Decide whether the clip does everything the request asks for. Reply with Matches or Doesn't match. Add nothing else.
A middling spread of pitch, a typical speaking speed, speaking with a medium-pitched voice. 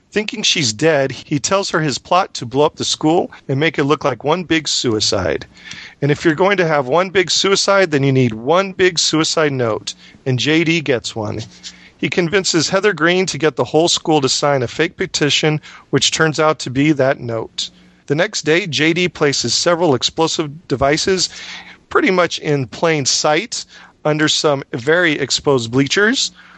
Matches